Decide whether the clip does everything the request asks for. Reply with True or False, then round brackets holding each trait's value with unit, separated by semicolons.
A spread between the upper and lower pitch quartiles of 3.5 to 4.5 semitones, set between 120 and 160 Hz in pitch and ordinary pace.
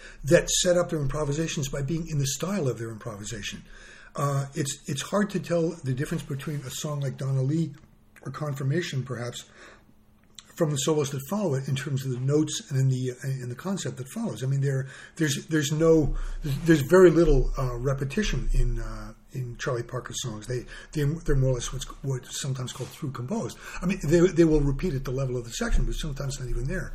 False (3.8 semitones; 140 Hz; 215 wpm)